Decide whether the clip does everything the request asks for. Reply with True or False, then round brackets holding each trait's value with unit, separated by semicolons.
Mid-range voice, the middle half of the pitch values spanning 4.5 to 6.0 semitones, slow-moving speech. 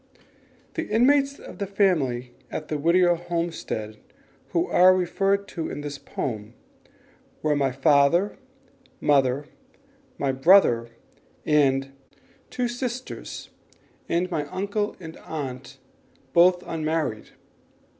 True (165 Hz; 5.4 semitones; 105 wpm)